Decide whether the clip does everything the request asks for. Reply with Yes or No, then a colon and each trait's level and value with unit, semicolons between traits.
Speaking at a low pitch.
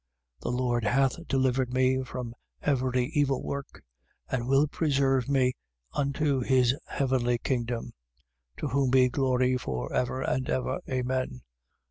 Yes: low, 130 Hz